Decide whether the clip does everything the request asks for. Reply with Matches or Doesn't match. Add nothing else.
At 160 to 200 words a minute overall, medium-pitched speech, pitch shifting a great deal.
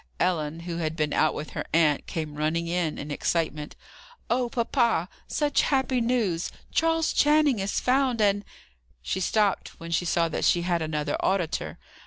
Matches